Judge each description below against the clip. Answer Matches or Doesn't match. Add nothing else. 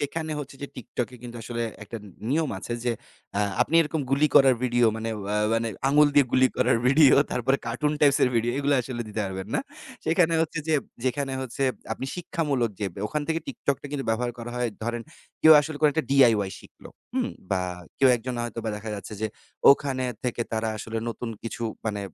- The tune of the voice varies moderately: Matches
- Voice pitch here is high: Doesn't match